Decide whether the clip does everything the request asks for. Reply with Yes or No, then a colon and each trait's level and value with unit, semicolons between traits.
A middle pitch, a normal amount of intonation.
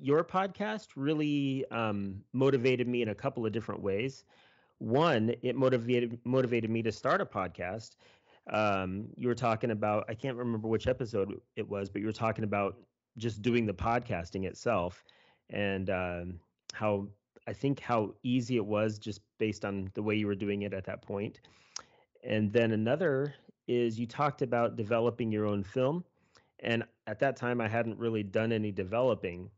No: low, 115 Hz; average, 3.3 semitones